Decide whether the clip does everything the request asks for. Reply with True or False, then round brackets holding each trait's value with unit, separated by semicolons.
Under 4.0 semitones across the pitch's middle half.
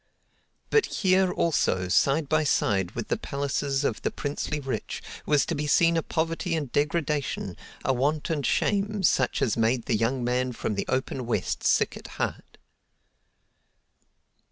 False (4.6 semitones)